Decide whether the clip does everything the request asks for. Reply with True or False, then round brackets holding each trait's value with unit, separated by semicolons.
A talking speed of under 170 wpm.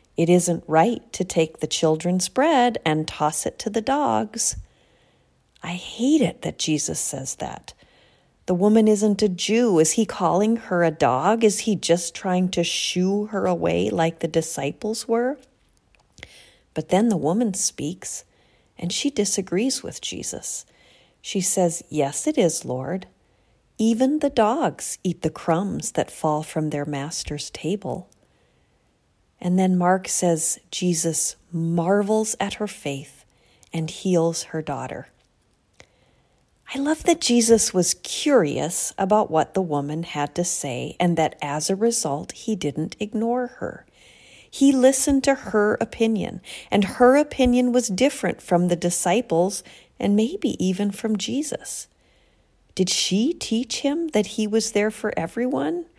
True (145 wpm)